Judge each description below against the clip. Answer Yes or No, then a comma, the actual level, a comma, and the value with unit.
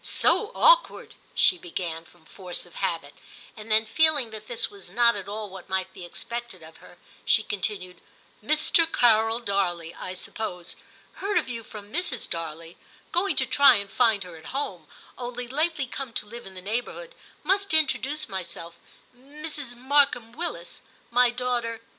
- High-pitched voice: Yes, high, 225 Hz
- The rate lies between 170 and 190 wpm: Yes, average, 185 wpm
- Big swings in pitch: Yes, wide, 5.9 semitones